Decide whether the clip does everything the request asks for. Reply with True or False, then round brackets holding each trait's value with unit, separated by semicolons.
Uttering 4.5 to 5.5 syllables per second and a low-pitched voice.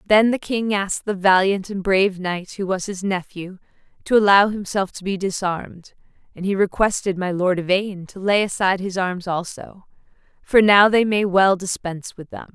False (5.0 syllables/s; 195 Hz)